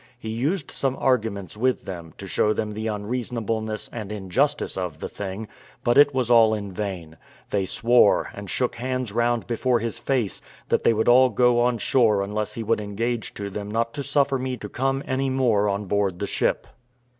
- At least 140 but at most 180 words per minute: No, average, 195 wpm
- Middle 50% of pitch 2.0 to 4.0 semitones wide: Yes, average, 3.6 semitones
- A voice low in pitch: Yes, low, 115 Hz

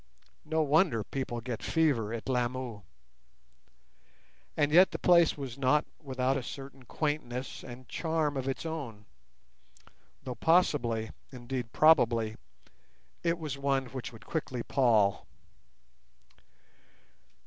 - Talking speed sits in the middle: No, slow, 105 wpm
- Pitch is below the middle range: Yes, low, 130 Hz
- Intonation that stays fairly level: No, average, 4.1 semitones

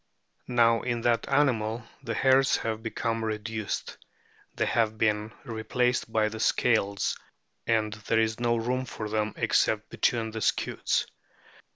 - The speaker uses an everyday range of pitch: No, narrow, 1.6 semitones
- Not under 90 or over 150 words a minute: Yes, average, 145 wpm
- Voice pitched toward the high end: No, low, 115 Hz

